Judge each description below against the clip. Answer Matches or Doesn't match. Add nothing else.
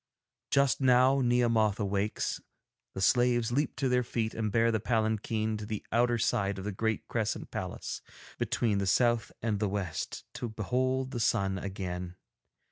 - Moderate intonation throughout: Matches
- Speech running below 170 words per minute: Matches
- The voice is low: Matches